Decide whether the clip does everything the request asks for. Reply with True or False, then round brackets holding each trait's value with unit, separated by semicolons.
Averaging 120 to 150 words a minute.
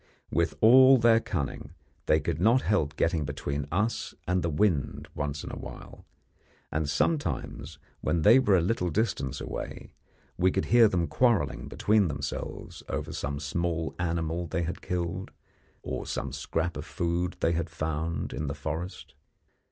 False (160 wpm)